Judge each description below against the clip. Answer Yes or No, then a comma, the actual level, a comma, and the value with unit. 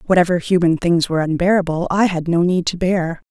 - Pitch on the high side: No, medium, 175 Hz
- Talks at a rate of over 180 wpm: Yes, average, 200 wpm